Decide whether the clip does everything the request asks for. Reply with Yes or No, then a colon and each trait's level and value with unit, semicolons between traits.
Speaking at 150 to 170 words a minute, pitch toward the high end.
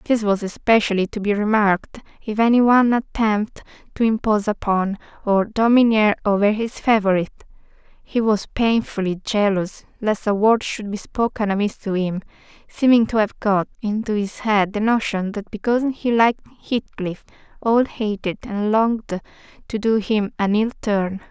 Yes: average, 155 wpm; high, 215 Hz